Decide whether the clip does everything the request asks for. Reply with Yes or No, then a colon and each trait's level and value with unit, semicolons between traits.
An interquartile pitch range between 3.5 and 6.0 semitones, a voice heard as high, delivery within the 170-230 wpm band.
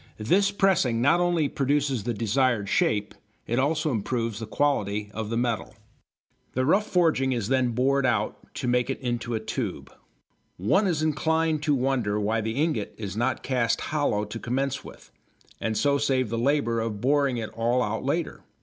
No: average, 4.3 semitones; low, 125 Hz; average, 175 wpm